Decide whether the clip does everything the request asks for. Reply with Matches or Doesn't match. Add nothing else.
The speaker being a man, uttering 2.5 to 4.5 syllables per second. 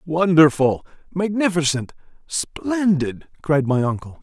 Matches